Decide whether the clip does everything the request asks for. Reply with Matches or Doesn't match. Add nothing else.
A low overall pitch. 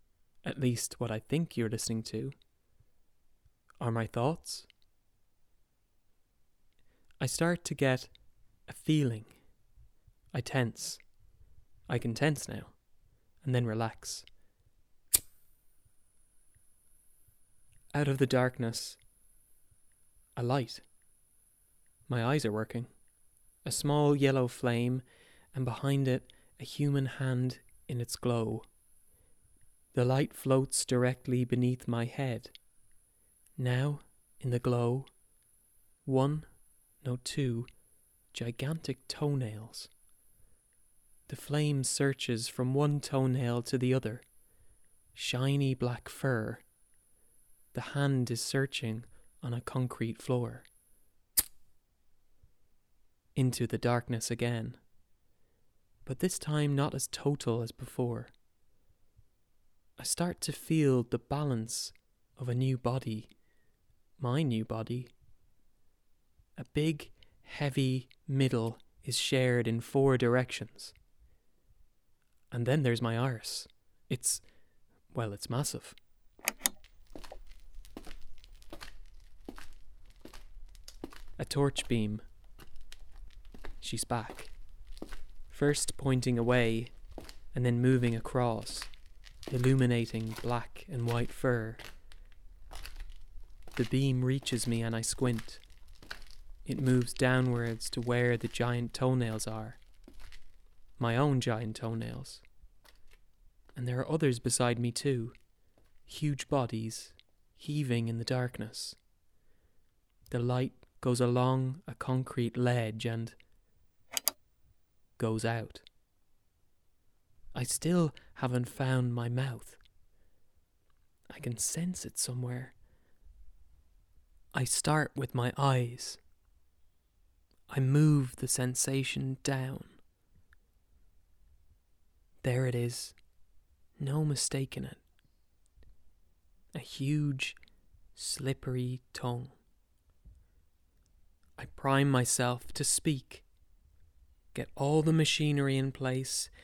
Matches